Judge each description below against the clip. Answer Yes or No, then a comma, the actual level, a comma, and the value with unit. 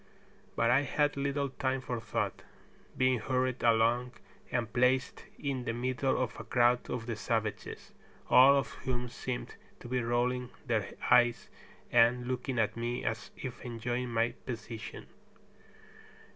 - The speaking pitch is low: Yes, low, 125 Hz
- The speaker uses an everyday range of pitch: No, narrow, 1.7 semitones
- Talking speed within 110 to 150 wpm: Yes, average, 145 wpm